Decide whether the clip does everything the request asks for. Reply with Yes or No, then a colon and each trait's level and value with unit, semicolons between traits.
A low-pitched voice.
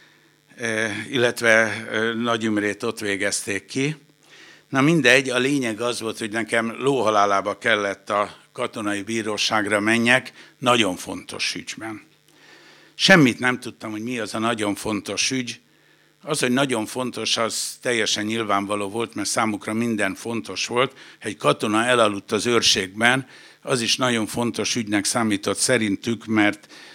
Yes: low, 115 Hz